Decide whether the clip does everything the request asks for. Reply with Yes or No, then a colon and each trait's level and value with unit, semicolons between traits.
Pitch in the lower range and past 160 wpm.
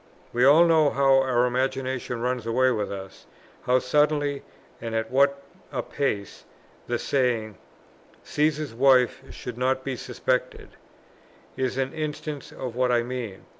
No: low, 130 Hz; average, 140 wpm